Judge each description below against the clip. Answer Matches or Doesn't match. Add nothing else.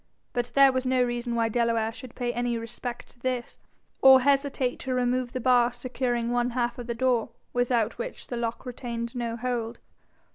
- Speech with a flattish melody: Matches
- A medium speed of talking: Matches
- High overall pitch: Matches